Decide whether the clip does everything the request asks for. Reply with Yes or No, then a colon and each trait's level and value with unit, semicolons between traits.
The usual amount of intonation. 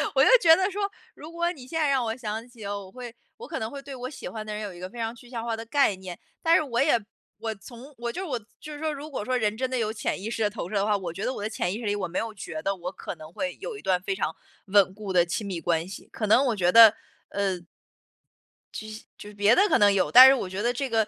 Yes: average, 4.6 semitones